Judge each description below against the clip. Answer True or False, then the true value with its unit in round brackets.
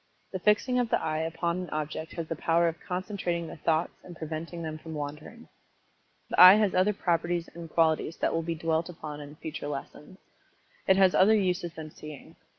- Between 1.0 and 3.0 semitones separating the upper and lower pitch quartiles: True (2.6 semitones)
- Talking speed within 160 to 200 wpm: True (195 wpm)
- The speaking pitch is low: False (165 Hz)